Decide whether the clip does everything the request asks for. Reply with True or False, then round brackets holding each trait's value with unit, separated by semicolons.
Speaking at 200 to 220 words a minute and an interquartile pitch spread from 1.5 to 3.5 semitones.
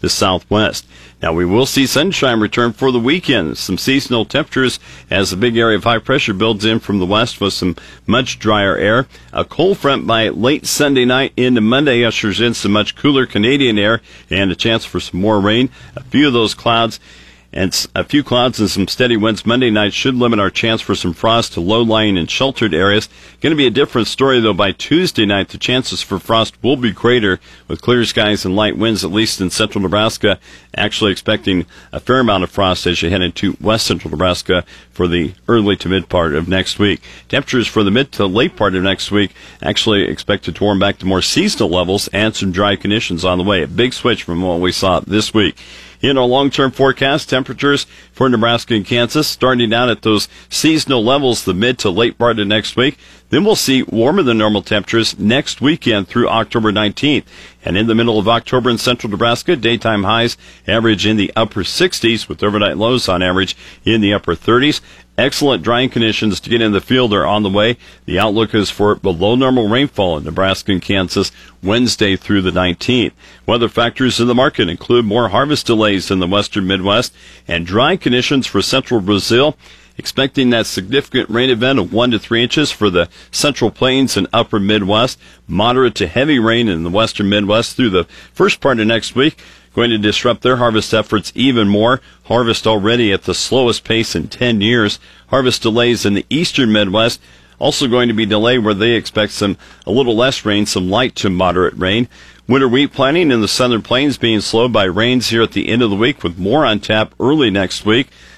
False (205 wpm; 3.9 semitones)